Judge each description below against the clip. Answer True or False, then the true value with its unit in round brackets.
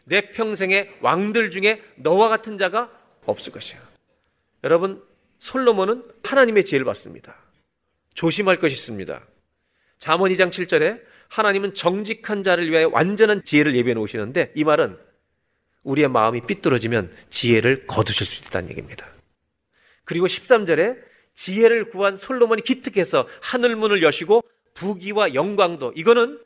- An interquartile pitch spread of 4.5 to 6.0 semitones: True (5.4 semitones)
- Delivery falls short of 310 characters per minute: False (315 characters per minute)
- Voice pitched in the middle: False (195 Hz)